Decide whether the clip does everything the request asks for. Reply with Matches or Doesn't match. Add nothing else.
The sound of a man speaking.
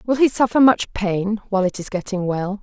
Doesn't match